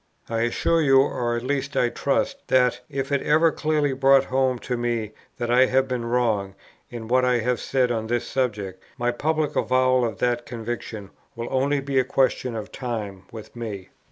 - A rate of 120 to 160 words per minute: No, average, 195 wpm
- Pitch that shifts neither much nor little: No, narrow, 2.3 semitones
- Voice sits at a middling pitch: No, low, 125 Hz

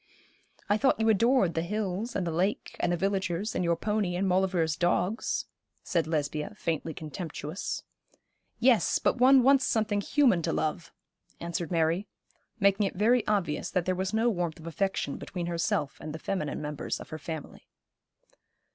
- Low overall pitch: No, medium, 185 Hz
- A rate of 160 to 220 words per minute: Yes, average, 165 wpm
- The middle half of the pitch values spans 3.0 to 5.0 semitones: Yes, average, 4.2 semitones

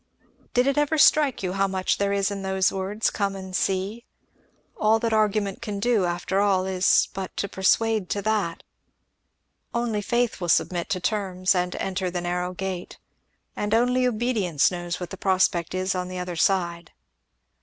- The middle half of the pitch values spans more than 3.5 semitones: No, average, 2.8 semitones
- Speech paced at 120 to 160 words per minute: No, average, 175 wpm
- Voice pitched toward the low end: No, high, 195 Hz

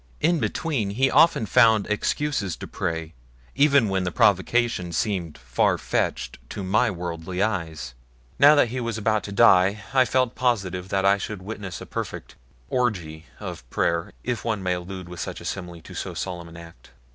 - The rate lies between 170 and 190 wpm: Yes, average, 180 wpm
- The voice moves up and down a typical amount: Yes, average, 4.9 semitones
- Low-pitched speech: Yes, low, 100 Hz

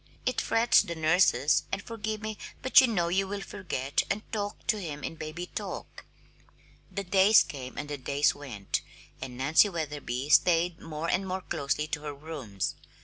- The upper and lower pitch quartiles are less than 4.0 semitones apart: No, wide, 5.4 semitones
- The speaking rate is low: No, average, 175 wpm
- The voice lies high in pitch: No, medium, 165 Hz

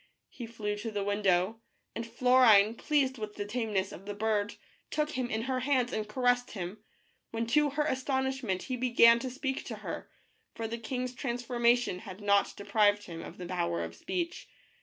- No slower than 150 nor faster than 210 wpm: Yes, average, 185 wpm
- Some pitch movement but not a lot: Yes, average, 3.7 semitones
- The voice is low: No, high, 230 Hz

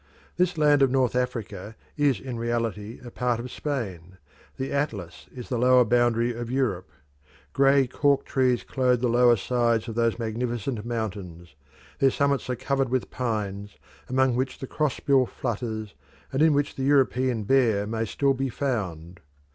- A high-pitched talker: No, low, 120 Hz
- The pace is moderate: Yes, average, 165 wpm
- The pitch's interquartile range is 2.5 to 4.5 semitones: Yes, average, 3.2 semitones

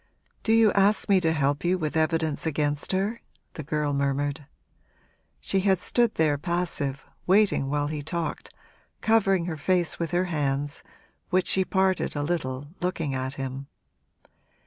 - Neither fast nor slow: Yes, average, 150 wpm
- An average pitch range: Yes, average, 4.4 semitones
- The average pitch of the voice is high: No, medium, 160 Hz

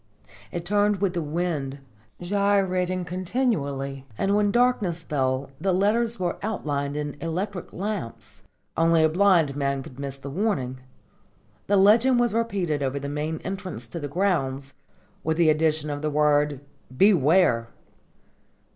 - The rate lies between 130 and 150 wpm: Yes, average, 140 wpm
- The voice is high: No, medium, 165 Hz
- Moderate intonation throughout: No, wide, 5.8 semitones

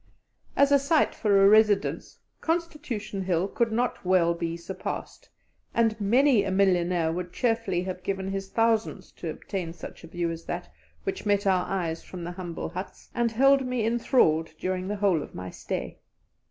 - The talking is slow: No, average, 175 wpm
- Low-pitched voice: No, high, 195 Hz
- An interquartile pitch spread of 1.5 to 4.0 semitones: No, average, 4.5 semitones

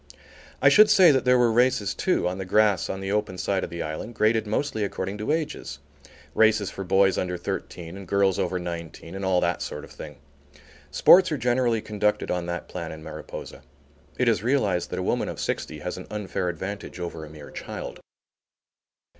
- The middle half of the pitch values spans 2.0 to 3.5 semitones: No, average, 4.0 semitones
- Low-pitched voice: Yes, very low, 95 Hz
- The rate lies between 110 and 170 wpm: No, average, 195 wpm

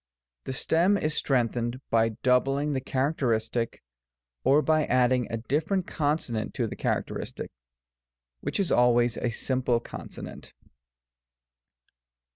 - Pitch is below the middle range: Yes, low, 130 Hz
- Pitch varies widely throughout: No, average, 3.8 semitones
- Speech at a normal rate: No, slow, 110 wpm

